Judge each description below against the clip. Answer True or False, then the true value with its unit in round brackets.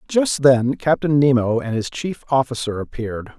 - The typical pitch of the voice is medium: False (130 Hz)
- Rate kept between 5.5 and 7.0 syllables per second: False (4.7 syllables/s)